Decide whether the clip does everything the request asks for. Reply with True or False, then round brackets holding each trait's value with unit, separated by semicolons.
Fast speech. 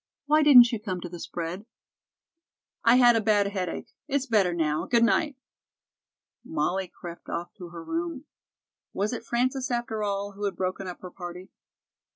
False (170 wpm)